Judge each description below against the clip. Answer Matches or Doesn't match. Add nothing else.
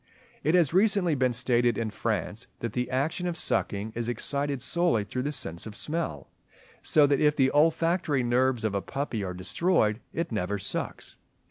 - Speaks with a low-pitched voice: Matches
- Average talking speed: Matches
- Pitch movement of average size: Doesn't match